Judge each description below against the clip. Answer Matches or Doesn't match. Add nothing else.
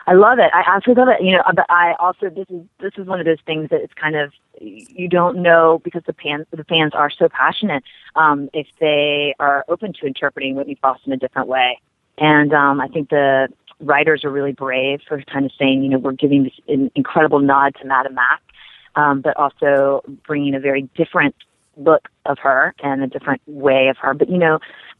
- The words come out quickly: Matches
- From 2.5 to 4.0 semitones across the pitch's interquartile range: Matches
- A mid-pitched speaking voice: Matches